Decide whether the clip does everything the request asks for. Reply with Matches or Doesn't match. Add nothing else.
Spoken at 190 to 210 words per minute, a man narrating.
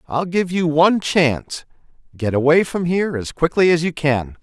Doesn't match